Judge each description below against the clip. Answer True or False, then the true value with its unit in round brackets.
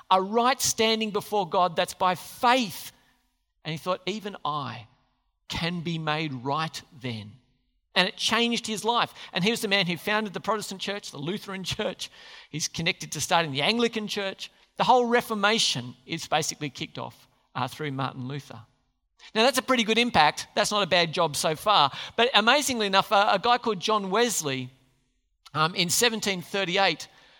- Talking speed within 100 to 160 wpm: False (175 wpm)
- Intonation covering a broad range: True (6.5 semitones)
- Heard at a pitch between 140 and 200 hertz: True (185 Hz)